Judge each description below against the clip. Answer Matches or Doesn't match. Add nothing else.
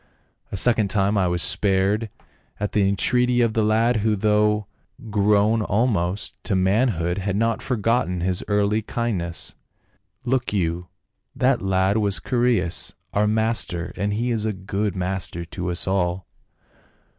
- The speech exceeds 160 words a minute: Doesn't match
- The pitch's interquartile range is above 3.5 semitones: Doesn't match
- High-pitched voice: Doesn't match